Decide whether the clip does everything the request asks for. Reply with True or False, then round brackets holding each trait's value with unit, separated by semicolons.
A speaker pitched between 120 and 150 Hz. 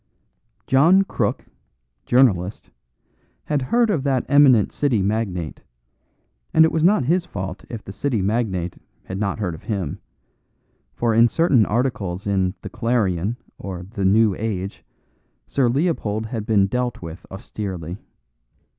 False (110 Hz)